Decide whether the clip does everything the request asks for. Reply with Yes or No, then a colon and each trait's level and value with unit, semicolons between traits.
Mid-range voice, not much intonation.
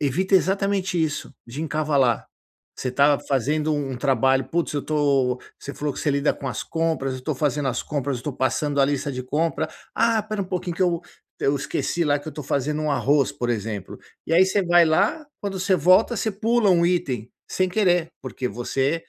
No: medium, 150 Hz; average, 4.6 semitones